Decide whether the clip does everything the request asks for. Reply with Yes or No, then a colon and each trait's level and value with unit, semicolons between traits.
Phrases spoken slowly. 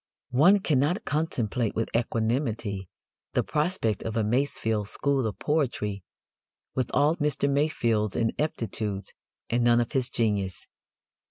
Yes: slow, 120 wpm